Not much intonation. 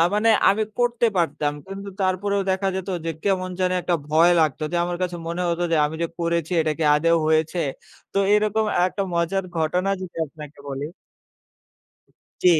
No: average, 3.4 semitones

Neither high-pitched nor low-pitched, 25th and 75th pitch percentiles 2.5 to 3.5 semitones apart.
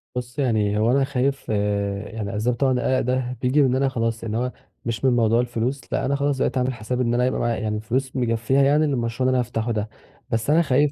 No: low, 125 Hz; average, 2.8 semitones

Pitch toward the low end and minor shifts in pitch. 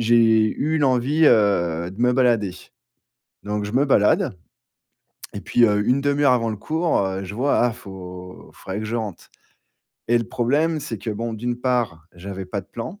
No: low, 115 Hz; average, 4.1 semitones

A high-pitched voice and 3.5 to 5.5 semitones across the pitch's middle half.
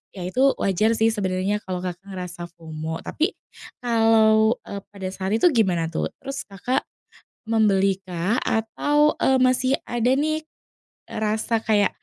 Yes: high, 215 Hz; average, 4.2 semitones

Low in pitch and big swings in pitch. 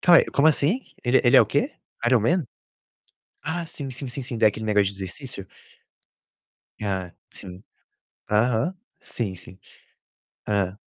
Yes: low, 120 Hz; wide, 6.2 semitones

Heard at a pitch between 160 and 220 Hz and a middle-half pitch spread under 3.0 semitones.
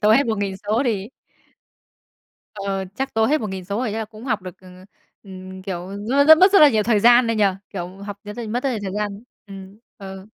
No: high, 210 Hz; average, 3.5 semitones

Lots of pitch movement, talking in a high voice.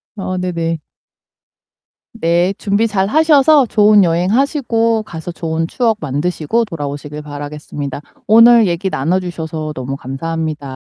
No: wide, 5.9 semitones; medium, 175 Hz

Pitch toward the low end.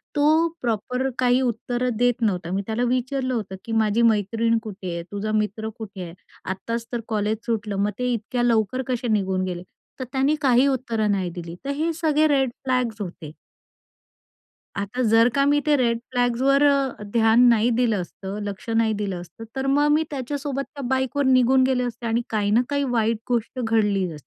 No: high, 230 Hz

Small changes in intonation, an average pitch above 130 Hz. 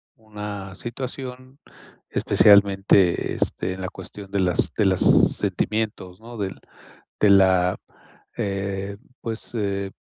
No: narrow, 2.2 semitones; low, 100 Hz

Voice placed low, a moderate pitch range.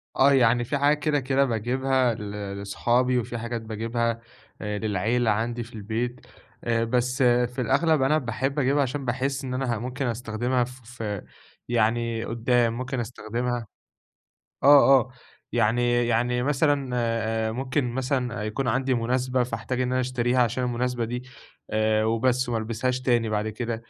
No: low, 120 Hz; narrow, 2.0 semitones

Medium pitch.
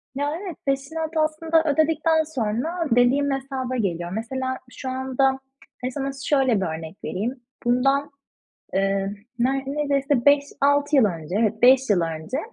No: very high, 265 Hz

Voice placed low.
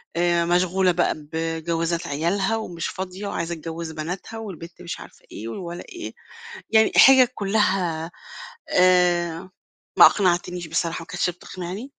No: medium, 175 Hz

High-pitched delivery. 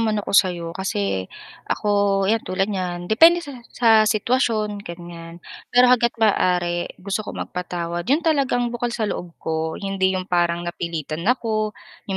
Yes: high, 195 Hz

